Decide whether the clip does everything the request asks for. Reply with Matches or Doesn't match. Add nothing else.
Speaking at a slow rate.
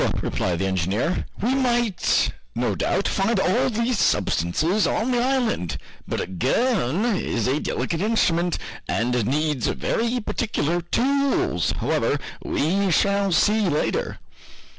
Matches